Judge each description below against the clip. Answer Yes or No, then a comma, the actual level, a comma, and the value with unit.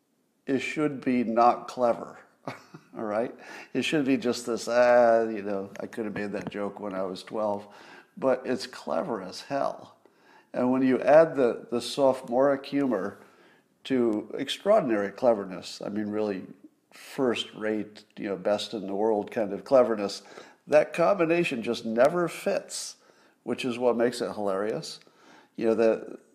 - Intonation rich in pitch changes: No, average, 3.7 semitones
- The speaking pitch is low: Yes, low, 115 Hz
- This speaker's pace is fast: No, average, 160 wpm